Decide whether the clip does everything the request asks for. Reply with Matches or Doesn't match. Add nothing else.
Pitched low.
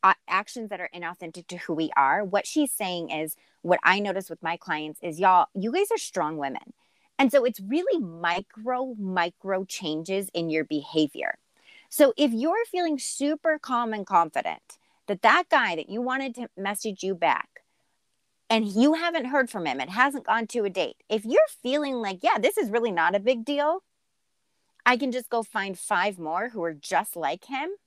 Doesn't match